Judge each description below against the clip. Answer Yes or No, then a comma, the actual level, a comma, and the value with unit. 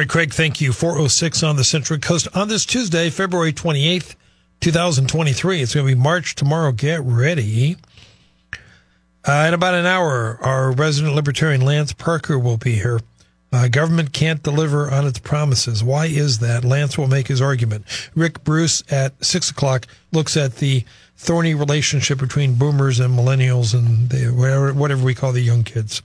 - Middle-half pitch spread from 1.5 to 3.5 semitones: No, average, 4.1 semitones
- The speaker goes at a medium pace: Yes, average, 170 wpm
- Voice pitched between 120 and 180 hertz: Yes, medium, 140 Hz